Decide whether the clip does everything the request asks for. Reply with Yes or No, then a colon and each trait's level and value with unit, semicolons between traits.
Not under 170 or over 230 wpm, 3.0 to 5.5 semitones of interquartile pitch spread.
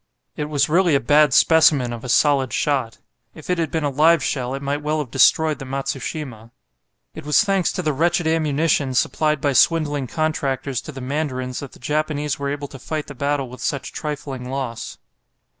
No: average, 195 wpm; narrow, 2.6 semitones